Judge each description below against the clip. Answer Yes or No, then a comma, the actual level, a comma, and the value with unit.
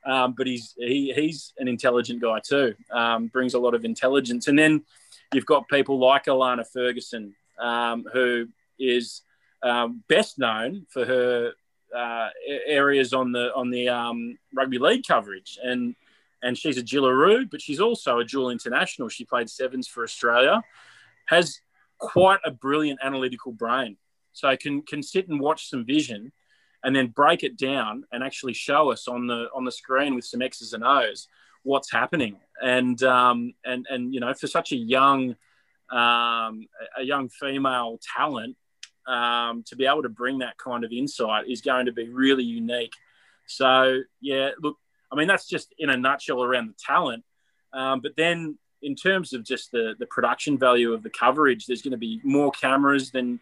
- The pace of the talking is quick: No, average, 175 wpm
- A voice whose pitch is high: No, low, 130 Hz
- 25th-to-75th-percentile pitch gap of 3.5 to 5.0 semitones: No, narrow, 2.4 semitones